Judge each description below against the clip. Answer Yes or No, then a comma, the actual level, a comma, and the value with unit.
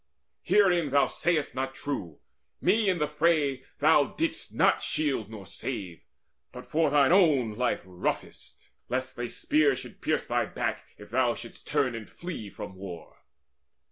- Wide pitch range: Yes, wide, 5.7 semitones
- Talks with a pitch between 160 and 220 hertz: No, low, 135 Hz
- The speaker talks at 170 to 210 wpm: No, average, 155 wpm